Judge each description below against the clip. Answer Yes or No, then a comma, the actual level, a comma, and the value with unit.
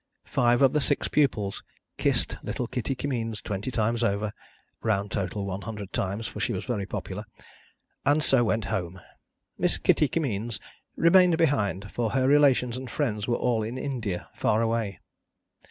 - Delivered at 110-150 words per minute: No, average, 160 wpm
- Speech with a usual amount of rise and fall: Yes, average, 4.3 semitones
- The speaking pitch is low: Yes, low, 115 Hz